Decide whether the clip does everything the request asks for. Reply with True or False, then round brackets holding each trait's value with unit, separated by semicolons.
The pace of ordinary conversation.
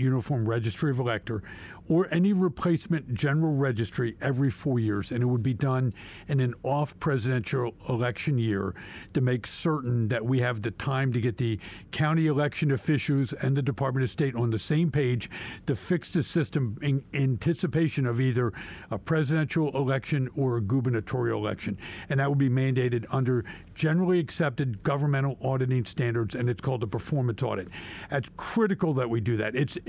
True (170 wpm)